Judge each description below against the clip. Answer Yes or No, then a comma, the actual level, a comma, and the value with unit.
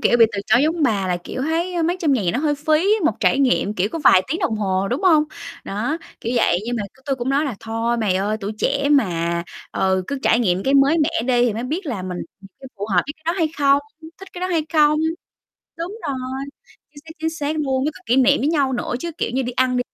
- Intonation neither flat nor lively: No, wide, 5.8 semitones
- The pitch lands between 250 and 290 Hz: Yes, very high, 265 Hz